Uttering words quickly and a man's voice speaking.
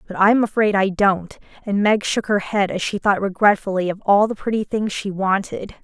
No: fast, 225 wpm; female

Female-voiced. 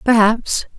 Yes: female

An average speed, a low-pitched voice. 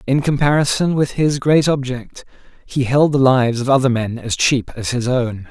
Yes: average, 195 wpm; low, 130 Hz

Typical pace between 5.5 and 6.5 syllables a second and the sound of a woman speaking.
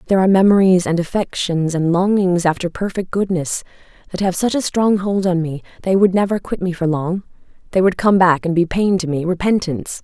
Yes: 5.7 syllables/s; female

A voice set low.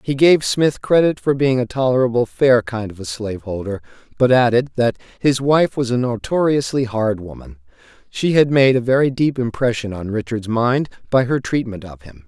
Yes: low, 120 Hz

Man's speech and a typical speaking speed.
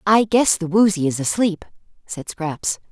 No: female; average, 165 wpm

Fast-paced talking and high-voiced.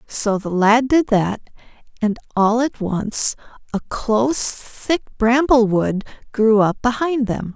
No: average, 145 wpm; high, 230 Hz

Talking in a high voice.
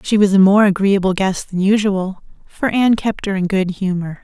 Yes: high, 195 Hz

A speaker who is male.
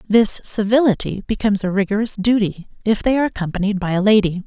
No: female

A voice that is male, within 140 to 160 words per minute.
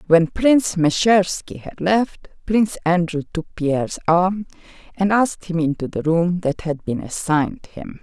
No: female; average, 155 wpm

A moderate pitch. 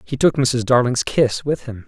No: low, 125 Hz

